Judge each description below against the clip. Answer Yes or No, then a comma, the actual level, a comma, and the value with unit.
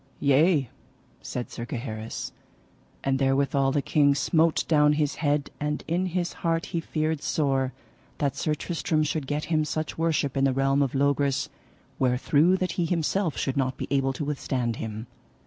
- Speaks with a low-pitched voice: No, medium, 145 Hz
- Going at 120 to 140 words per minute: No, average, 165 wpm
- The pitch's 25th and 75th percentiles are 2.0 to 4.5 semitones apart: Yes, average, 2.8 semitones